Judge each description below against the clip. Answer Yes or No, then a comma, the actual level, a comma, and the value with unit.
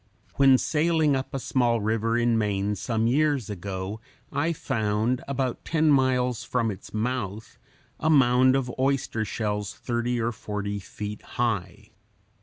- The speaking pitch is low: Yes, low, 120 Hz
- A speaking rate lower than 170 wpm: Yes, average, 140 wpm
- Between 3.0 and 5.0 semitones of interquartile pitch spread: Yes, average, 4.0 semitones